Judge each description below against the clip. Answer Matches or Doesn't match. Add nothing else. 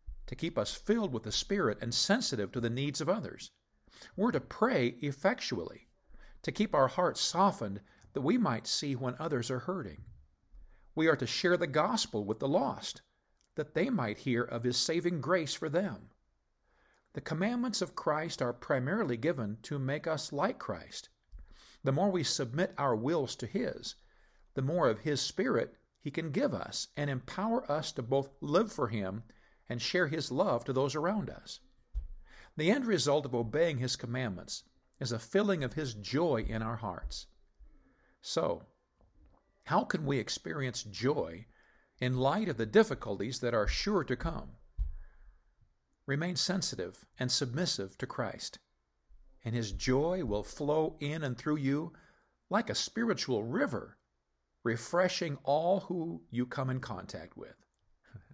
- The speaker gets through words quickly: Doesn't match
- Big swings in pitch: Matches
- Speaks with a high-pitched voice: Doesn't match